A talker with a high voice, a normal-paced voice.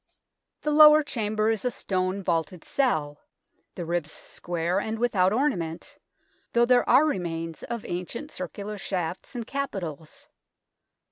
No: high, 195 Hz; slow, 130 wpm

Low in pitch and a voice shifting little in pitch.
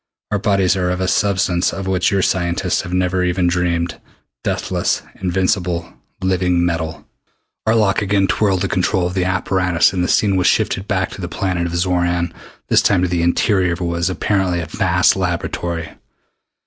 Yes: very low, 90 Hz; narrow, 1.6 semitones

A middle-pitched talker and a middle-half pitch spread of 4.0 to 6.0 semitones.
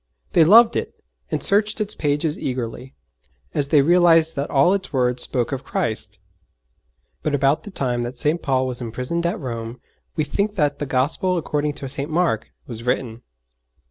Yes: medium, 145 Hz; average, 5.0 semitones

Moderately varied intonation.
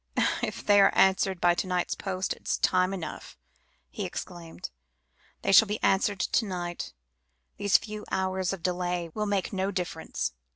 No: narrow, 1.9 semitones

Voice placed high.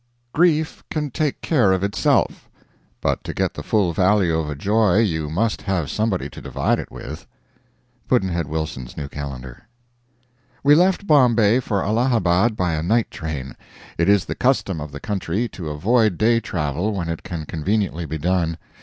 No: very low, 95 Hz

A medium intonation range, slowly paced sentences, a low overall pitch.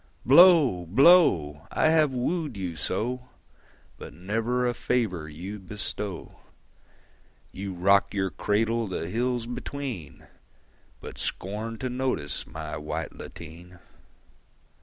No: wide, 5.9 semitones; slow, 110 wpm; low, 105 Hz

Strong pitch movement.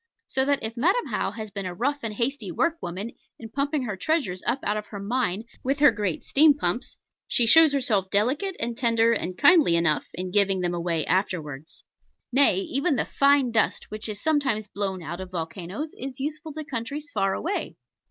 Yes: wide, 6.8 semitones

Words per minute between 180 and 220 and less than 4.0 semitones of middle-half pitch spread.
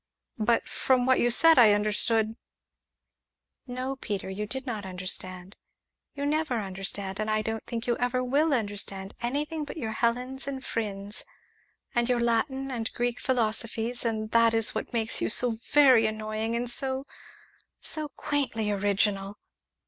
No: average, 155 wpm; average, 3.3 semitones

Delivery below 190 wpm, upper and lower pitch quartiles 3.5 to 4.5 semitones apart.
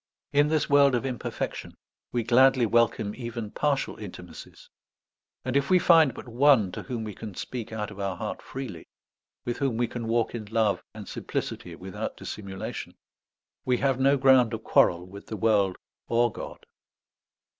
Yes: average, 165 wpm; average, 4.0 semitones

